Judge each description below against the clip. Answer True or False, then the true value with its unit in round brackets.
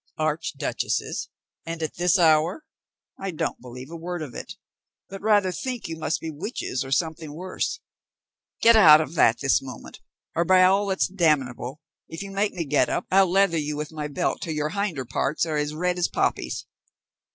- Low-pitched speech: False (165 Hz)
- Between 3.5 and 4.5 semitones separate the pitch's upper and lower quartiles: True (3.8 semitones)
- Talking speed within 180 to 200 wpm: True (185 wpm)